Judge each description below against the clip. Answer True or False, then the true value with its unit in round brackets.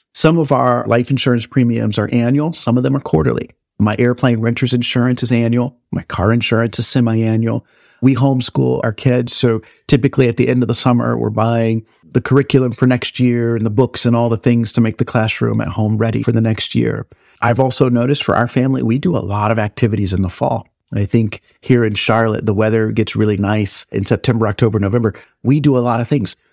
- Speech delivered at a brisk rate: True (220 wpm)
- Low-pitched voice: True (120 Hz)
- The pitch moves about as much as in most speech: False (2.2 semitones)